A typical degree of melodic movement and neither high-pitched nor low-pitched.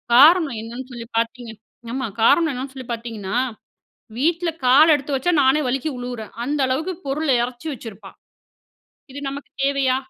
No: average, 3.1 semitones; very high, 260 Hz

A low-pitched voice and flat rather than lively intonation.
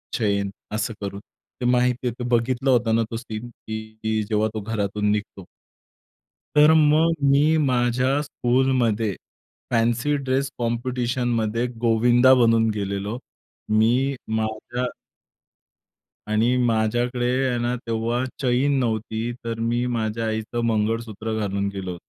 Yes: low, 115 Hz; narrow, 2.2 semitones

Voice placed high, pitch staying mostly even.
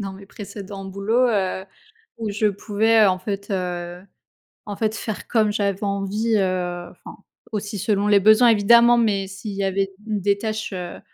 Yes: high, 200 Hz; narrow, 2.0 semitones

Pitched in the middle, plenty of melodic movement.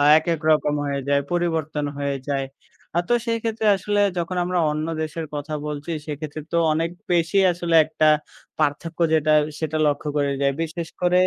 No: medium, 155 Hz; average, 2.8 semitones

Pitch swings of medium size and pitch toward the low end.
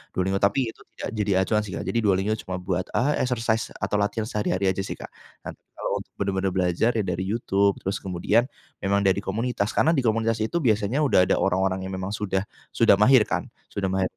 Yes: average, 3.0 semitones; low, 100 Hz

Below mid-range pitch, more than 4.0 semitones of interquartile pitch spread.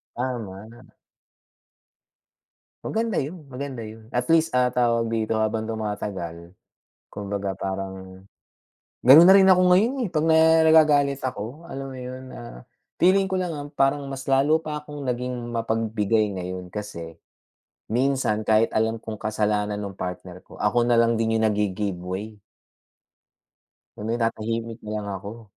Yes: low, 115 Hz; average, 4.6 semitones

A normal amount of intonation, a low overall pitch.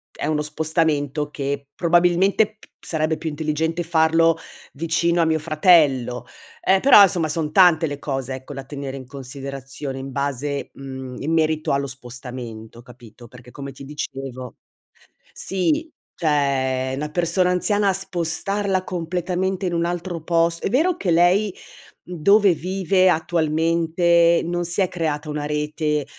No: average, 4.0 semitones; medium, 160 Hz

